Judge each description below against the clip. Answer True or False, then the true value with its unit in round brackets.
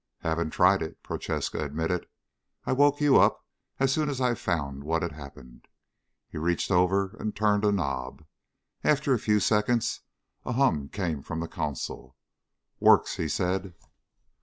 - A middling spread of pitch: False (5.8 semitones)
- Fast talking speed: False (155 wpm)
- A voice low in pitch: True (90 Hz)